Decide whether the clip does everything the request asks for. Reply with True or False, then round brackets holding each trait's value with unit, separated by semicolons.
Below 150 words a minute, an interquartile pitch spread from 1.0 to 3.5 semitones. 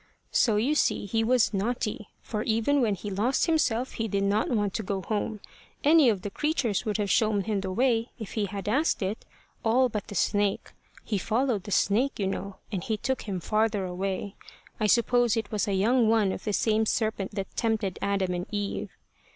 False (205 wpm; 2.7 semitones)